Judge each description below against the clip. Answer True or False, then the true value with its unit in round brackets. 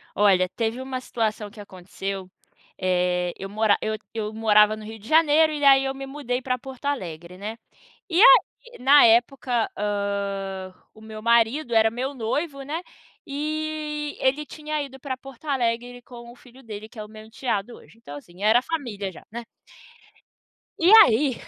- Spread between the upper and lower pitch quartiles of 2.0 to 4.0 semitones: False (4.6 semitones)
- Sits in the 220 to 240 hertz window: True (235 Hz)